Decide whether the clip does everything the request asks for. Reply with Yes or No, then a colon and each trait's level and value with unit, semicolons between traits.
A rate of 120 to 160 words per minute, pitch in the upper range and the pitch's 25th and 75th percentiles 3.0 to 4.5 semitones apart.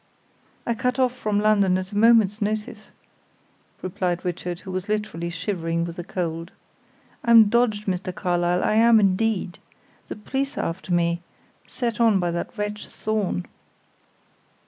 Yes: average, 145 wpm; high, 200 Hz; average, 3.6 semitones